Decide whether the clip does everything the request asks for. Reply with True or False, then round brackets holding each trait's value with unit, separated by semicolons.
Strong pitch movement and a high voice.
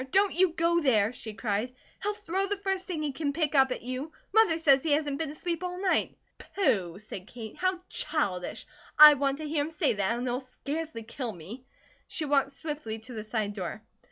True (6.2 semitones; 280 Hz)